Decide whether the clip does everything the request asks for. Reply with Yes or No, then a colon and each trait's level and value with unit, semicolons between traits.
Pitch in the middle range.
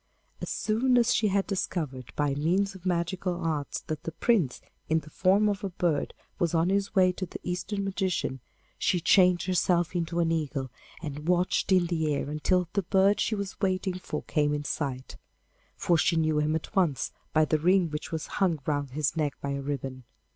Yes: medium, 170 Hz